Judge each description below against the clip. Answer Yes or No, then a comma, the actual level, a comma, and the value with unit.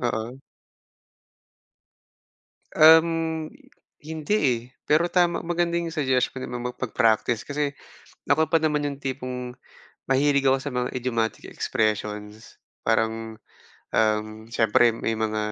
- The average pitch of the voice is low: Yes, low, 130 Hz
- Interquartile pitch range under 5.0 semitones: No, wide, 5.5 semitones